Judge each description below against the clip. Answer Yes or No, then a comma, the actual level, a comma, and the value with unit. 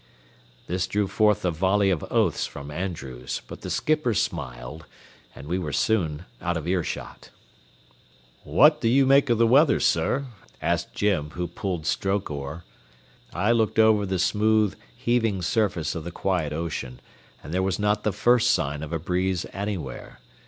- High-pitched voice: No, very low, 95 Hz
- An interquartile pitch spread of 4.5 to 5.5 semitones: Yes, average, 4.9 semitones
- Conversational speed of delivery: Yes, average, 165 wpm